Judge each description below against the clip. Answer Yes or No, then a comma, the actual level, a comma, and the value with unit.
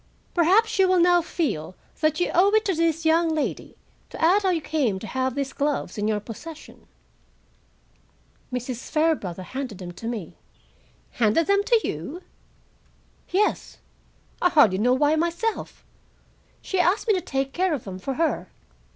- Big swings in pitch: Yes, wide, 6.7 semitones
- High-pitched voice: Yes, very high, 310 Hz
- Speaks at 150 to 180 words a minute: Yes, average, 160 wpm